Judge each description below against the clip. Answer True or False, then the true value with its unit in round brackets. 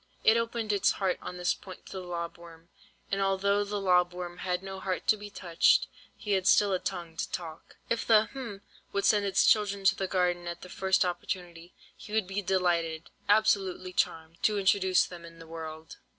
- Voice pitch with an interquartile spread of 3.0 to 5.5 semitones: False (2.4 semitones)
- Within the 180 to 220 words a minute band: True (195 wpm)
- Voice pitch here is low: False (185 Hz)